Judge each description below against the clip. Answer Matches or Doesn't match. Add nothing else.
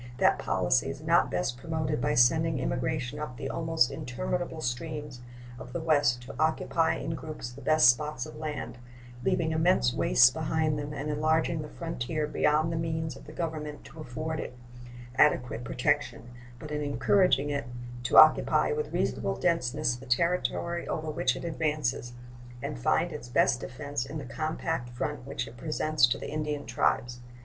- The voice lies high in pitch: Doesn't match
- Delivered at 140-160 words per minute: Doesn't match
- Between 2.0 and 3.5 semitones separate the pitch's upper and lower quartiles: Doesn't match